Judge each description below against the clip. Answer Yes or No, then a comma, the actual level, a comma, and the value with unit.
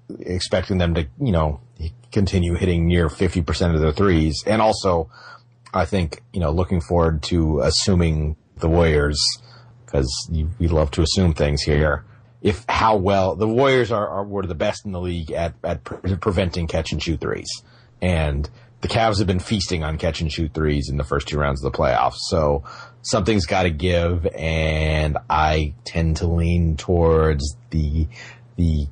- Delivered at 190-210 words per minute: No, average, 175 wpm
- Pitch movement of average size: Yes, average, 4.2 semitones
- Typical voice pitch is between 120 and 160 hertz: No, very low, 85 Hz